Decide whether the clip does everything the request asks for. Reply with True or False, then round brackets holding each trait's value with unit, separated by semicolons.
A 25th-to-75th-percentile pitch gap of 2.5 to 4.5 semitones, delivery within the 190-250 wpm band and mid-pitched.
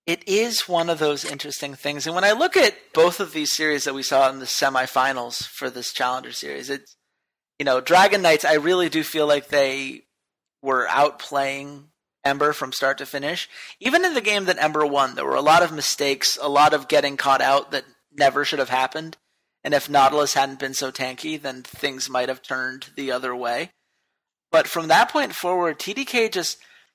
True (3.2 semitones; 200 wpm; 145 Hz)